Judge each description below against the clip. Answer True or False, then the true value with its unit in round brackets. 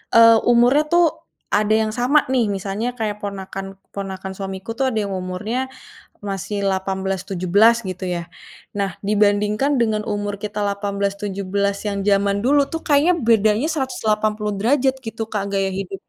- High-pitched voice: True (205 Hz)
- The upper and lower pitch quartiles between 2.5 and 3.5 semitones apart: True (2.8 semitones)